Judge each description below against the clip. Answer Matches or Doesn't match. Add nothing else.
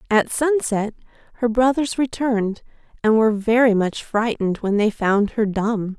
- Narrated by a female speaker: Matches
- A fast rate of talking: Doesn't match